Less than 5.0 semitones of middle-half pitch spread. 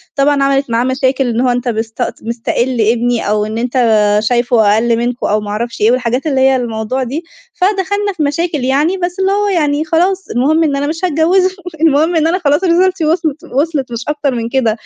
No: wide, 5.4 semitones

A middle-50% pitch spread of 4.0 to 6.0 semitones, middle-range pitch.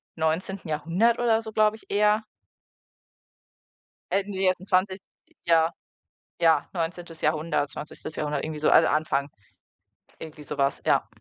Yes: average, 4.3 semitones; medium, 170 Hz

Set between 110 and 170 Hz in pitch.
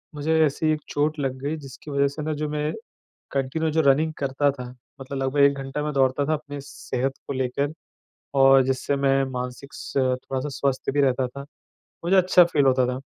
Yes: medium, 140 Hz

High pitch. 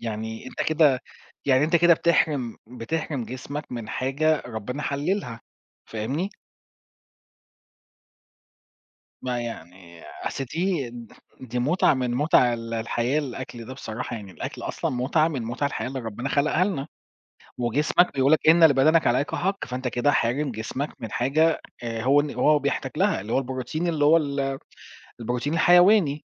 No: low, 135 Hz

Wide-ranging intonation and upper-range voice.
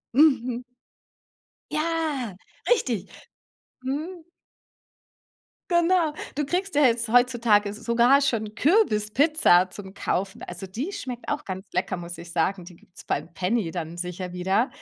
Yes: wide, 7.5 semitones; high, 230 Hz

